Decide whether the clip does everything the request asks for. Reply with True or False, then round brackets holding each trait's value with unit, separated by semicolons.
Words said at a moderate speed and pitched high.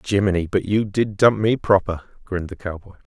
False (190 wpm; 100 Hz)